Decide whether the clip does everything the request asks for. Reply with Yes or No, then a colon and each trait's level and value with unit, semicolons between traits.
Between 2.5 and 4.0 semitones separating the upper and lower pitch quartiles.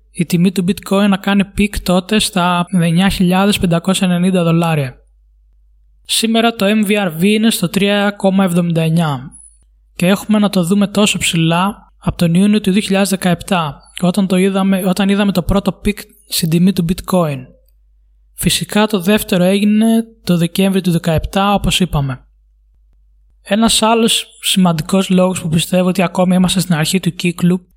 Yes: average, 2.9 semitones